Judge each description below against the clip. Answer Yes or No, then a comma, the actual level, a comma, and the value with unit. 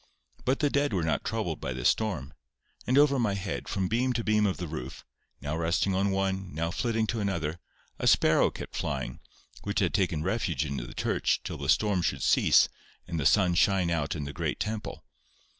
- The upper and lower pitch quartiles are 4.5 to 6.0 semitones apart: Yes, average, 4.9 semitones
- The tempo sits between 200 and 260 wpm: Yes, fast, 205 wpm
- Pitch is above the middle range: No, very low, 95 Hz